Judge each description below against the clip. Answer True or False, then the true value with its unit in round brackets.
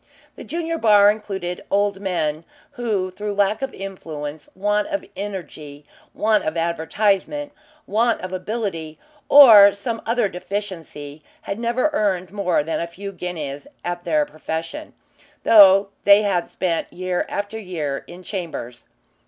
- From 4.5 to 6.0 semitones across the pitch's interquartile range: False (3.9 semitones)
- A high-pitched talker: True (195 Hz)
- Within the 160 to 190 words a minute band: False (135 wpm)